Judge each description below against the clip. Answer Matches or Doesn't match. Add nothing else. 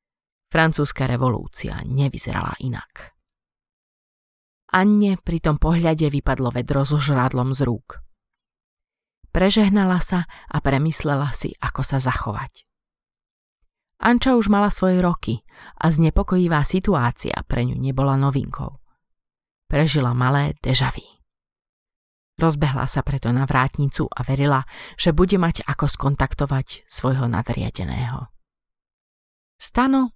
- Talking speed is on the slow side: Matches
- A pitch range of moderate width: Matches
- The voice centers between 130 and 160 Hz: Matches